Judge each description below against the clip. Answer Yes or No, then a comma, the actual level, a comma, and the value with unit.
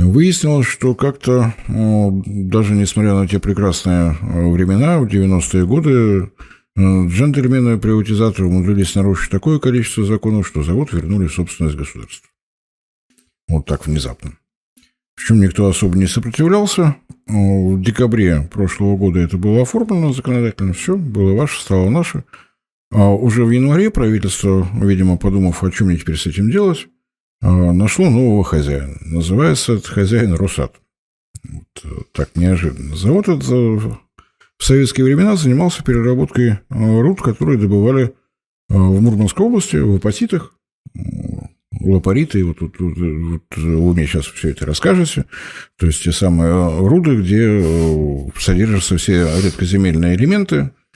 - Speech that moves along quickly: No, average, 125 wpm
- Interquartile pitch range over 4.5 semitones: Yes, average, 5.3 semitones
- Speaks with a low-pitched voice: Yes, low, 100 Hz